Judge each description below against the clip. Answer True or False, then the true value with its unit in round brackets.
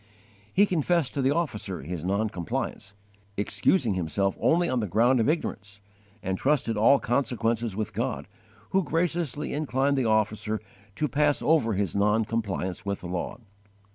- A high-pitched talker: False (115 Hz)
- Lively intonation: True (5.9 semitones)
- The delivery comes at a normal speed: True (155 wpm)